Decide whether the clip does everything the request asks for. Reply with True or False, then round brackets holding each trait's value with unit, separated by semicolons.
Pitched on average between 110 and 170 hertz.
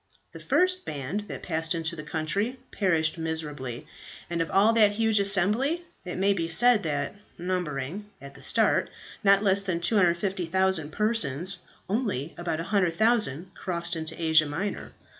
False (180 Hz)